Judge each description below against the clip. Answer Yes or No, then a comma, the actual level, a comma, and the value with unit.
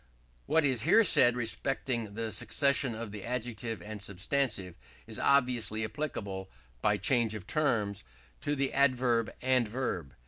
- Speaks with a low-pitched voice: Yes, low, 120 Hz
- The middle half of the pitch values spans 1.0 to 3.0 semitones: No, average, 3.7 semitones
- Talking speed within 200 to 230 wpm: No, average, 140 wpm